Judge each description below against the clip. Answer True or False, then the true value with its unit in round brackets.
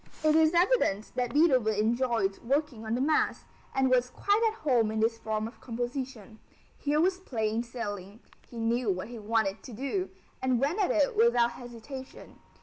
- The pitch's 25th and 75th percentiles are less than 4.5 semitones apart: True (4.1 semitones)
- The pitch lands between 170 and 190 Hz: False (240 Hz)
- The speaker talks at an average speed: True (175 wpm)